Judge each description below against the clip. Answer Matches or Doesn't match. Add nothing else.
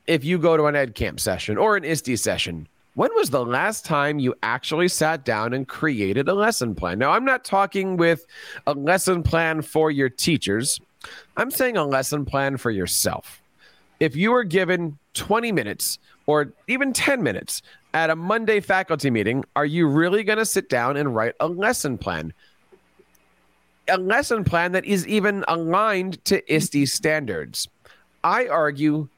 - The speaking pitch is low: Doesn't match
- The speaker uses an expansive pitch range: Matches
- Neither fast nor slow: Matches